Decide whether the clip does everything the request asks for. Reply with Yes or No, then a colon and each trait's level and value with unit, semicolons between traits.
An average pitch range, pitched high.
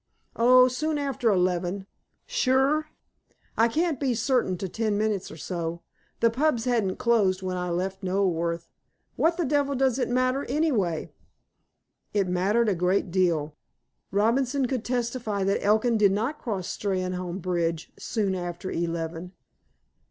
No: wide, 5.7 semitones; high, 205 Hz